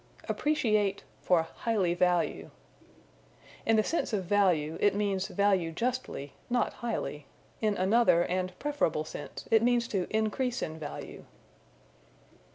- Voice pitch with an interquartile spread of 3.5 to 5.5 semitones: Yes, average, 4.6 semitones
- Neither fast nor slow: No, slow, 125 wpm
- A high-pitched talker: Yes, high, 200 Hz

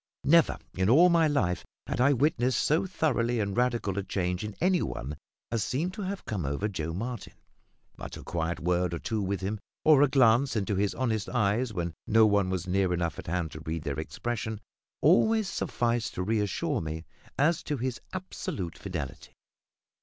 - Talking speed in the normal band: Yes, average, 185 wpm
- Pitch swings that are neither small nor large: No, wide, 6.4 semitones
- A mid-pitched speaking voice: No, low, 110 Hz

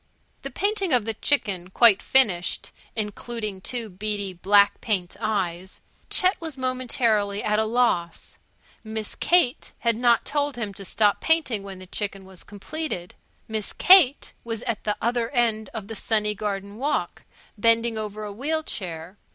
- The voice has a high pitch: Yes, high, 215 Hz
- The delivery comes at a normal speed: Yes, average, 155 wpm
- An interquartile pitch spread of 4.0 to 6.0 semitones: No, average, 3.5 semitones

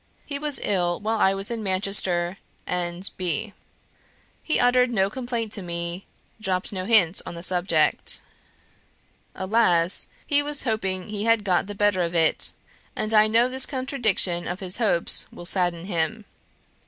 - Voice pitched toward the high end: Yes, high, 195 Hz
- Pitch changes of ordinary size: Yes, average, 4.1 semitones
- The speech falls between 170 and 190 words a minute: No, average, 160 wpm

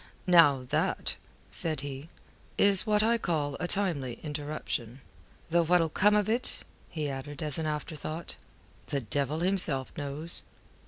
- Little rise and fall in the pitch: No, average, 3.9 semitones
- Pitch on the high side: No, medium, 155 Hz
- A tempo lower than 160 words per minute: Yes, average, 140 wpm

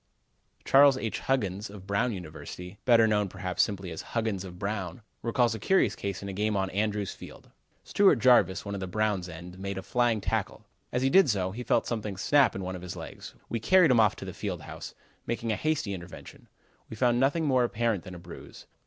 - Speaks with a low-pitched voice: Yes, low, 105 Hz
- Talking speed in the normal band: No, fast, 215 wpm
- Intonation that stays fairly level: No, average, 4.1 semitones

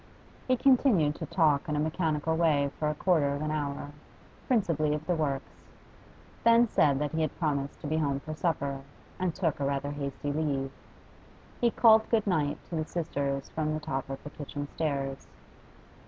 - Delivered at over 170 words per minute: Yes, average, 185 wpm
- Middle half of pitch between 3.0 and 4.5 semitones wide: No, narrow, 2.6 semitones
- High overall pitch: No, medium, 150 Hz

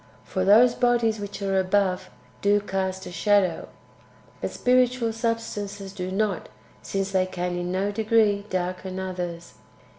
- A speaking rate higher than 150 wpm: No, average, 140 wpm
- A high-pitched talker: Yes, high, 195 Hz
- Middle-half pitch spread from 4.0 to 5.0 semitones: No, average, 2.7 semitones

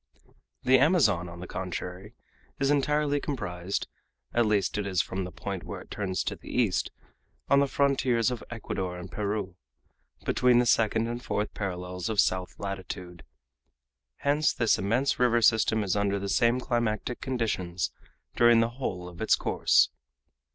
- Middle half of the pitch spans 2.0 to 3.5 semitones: No, average, 4.8 semitones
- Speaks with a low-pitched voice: Yes, low, 105 Hz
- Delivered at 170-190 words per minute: No, average, 160 wpm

